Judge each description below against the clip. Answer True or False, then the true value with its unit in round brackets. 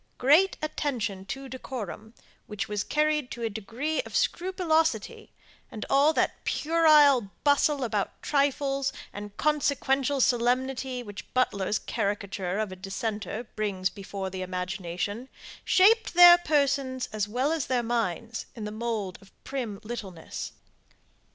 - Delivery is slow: True (130 wpm)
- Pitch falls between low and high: False (240 Hz)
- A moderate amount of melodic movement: False (5.8 semitones)